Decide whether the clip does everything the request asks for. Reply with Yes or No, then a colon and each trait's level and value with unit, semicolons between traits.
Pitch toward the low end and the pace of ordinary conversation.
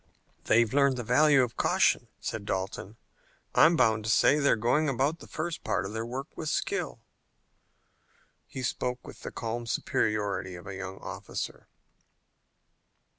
Yes: low, 120 Hz; average, 150 wpm